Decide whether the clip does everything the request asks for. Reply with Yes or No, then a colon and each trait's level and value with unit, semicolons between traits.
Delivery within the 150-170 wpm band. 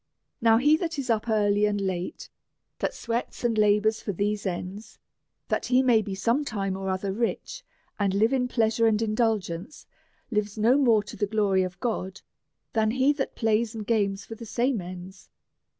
No: average, 180 wpm